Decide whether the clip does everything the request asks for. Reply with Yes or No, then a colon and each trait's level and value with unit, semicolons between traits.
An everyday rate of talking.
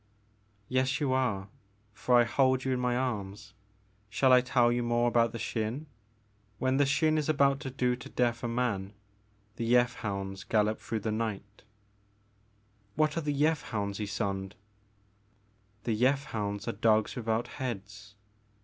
Yes: average, 165 wpm